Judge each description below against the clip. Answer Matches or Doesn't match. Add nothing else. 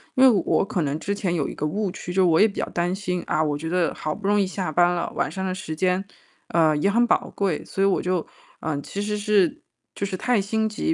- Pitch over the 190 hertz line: Doesn't match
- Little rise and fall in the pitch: Doesn't match